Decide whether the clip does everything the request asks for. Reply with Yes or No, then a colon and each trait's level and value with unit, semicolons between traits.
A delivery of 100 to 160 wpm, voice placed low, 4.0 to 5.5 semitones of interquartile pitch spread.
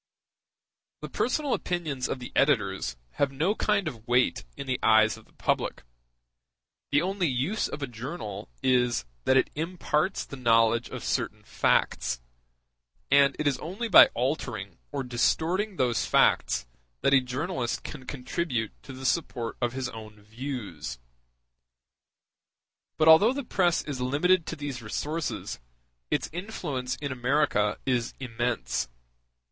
Yes: average, 140 wpm; low, 130 Hz; average, 5.1 semitones